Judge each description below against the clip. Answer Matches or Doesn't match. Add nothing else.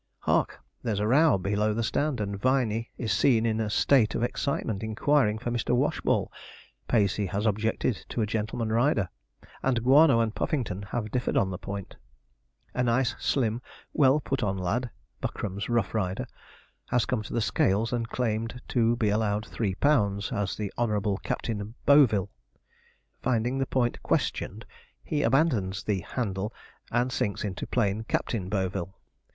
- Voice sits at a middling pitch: Doesn't match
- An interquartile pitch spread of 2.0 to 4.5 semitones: Matches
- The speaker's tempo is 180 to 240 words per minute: Doesn't match